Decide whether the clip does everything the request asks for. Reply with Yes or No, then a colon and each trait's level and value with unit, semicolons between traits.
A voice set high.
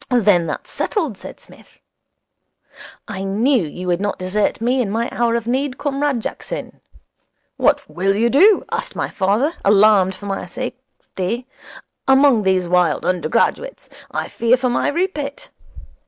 Yes: high, 230 Hz